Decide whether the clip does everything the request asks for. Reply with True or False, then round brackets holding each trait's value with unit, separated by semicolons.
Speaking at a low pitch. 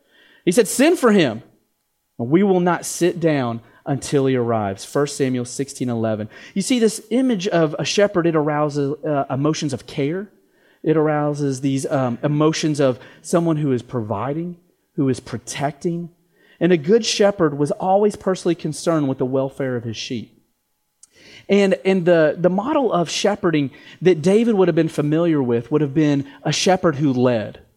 False (155 Hz)